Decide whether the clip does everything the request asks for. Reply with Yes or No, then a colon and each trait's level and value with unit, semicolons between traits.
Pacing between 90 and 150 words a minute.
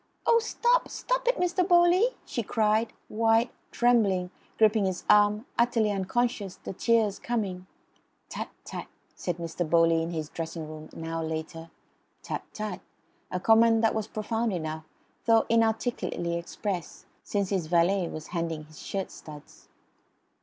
Yes: average, 145 wpm